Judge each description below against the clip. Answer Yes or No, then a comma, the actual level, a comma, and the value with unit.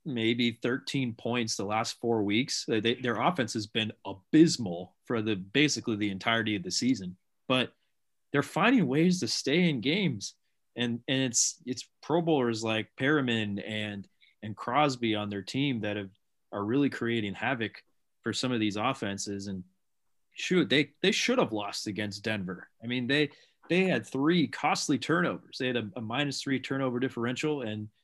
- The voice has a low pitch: Yes, low, 120 Hz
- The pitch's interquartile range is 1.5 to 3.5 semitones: No, average, 4.5 semitones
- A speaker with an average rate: Yes, average, 170 wpm